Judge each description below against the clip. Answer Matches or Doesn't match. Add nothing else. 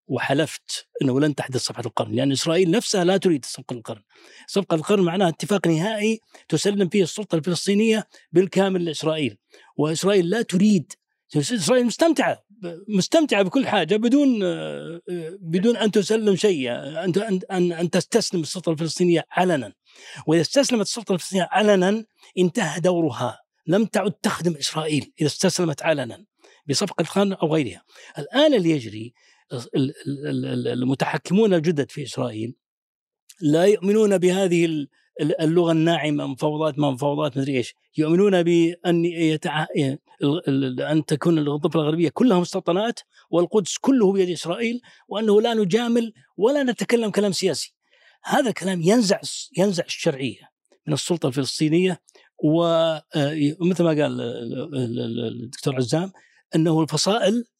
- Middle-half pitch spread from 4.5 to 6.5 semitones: Matches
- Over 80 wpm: Matches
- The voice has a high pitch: Doesn't match